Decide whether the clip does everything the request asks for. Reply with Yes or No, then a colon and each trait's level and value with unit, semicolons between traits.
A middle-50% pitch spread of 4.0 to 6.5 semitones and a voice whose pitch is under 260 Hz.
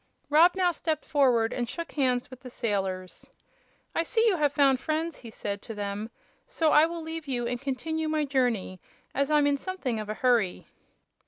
No: wide, 5.4 semitones; very high, 270 Hz